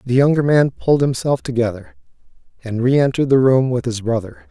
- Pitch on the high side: No, low, 130 Hz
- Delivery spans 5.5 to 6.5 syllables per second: Yes, 5.9 syllables/s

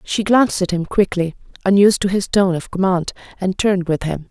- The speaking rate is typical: No, fast, 210 wpm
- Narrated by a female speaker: Yes, female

